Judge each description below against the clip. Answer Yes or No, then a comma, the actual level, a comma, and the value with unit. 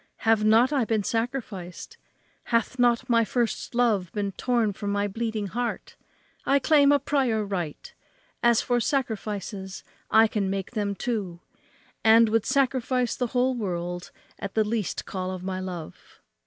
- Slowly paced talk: No, average, 155 wpm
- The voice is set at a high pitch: Yes, high, 220 Hz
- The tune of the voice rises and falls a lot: No, average, 3.7 semitones